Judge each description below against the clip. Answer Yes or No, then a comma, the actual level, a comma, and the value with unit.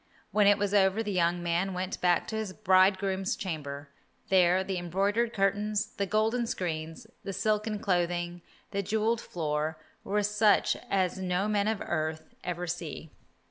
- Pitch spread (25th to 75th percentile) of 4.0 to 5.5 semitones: No, average, 3.1 semitones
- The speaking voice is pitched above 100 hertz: Yes, high, 190 Hz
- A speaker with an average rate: Yes, average, 155 wpm